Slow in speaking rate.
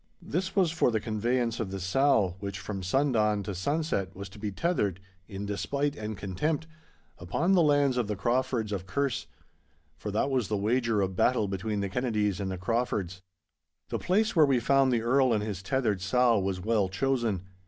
No: average, 190 wpm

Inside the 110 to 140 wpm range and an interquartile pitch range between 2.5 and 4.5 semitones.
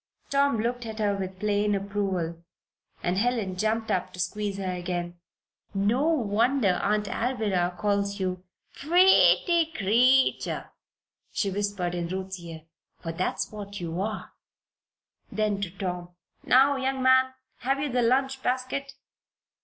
No: slow, 135 wpm; wide, 5.4 semitones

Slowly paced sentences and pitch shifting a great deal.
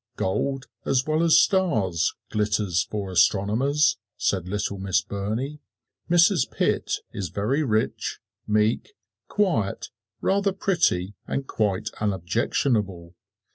Yes: slow, 105 wpm; wide, 6.9 semitones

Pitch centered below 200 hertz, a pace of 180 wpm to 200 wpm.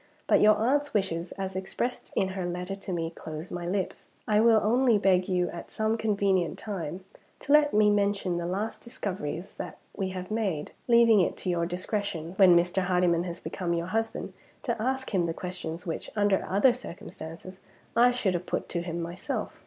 Yes: high, 190 Hz; average, 190 wpm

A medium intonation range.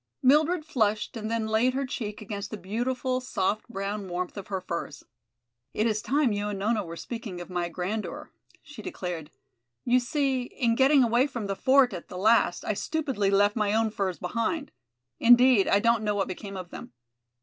Yes: average, 4.1 semitones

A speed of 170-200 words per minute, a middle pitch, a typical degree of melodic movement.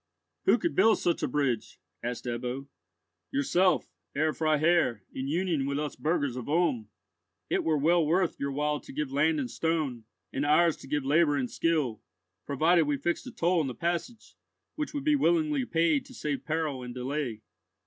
Yes: average, 180 wpm; medium, 150 Hz; average, 4.0 semitones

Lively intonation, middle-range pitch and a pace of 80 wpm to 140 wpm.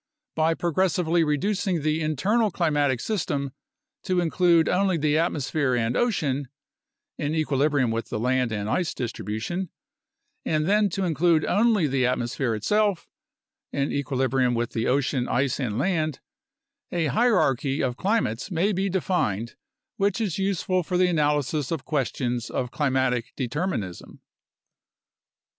Yes: wide, 5.8 semitones; medium, 150 Hz; slow, 135 wpm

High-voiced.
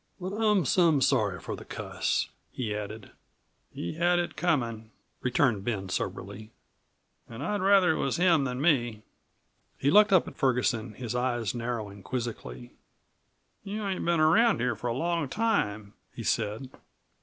No: low, 125 Hz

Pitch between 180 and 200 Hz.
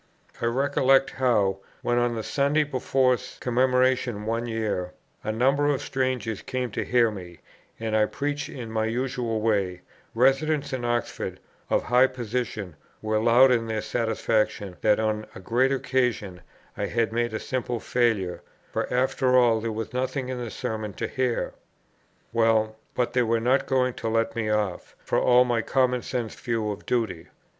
No: low, 120 Hz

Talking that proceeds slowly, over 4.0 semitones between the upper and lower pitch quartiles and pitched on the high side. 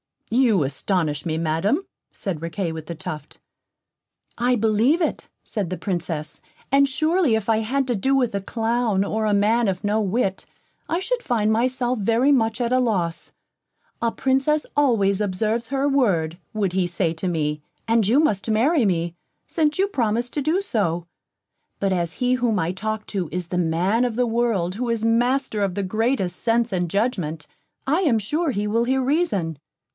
No: average, 180 wpm; wide, 5.4 semitones; high, 220 Hz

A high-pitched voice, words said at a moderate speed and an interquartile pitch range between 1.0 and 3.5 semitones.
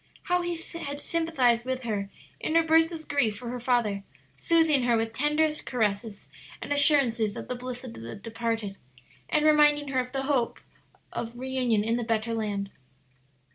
No: very high, 250 Hz; average, 175 wpm; average, 4.7 semitones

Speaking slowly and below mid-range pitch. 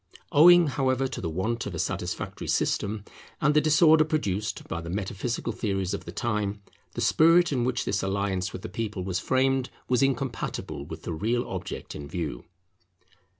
No: average, 175 wpm; low, 115 Hz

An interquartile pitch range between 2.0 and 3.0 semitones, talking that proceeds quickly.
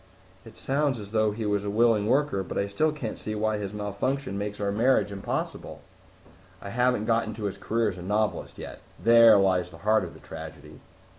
Yes: narrow, 2.6 semitones; fast, 210 wpm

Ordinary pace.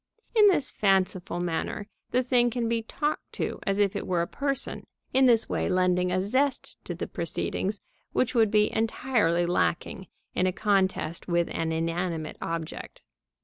Yes: average, 165 wpm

